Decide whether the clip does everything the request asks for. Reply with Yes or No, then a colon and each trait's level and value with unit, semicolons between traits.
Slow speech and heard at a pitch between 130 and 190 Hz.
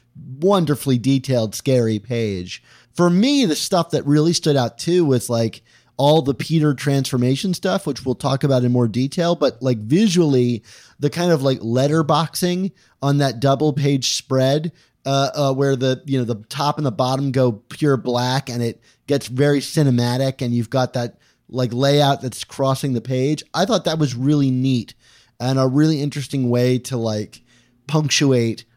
No: average, 175 wpm; low, 135 Hz